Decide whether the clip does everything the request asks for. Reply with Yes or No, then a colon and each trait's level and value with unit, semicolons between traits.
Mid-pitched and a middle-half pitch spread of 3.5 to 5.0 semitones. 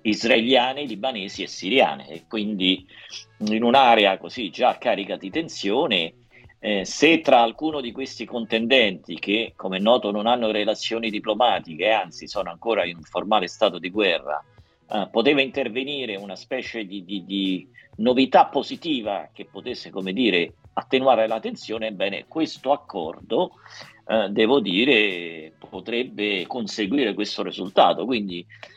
No: low, 110 Hz; average, 3.8 semitones